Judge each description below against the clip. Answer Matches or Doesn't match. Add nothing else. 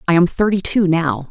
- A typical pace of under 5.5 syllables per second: Matches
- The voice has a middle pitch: Matches